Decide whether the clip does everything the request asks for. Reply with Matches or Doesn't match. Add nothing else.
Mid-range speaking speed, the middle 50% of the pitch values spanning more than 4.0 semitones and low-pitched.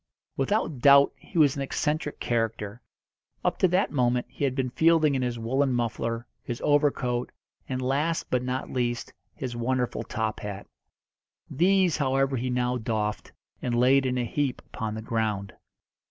Doesn't match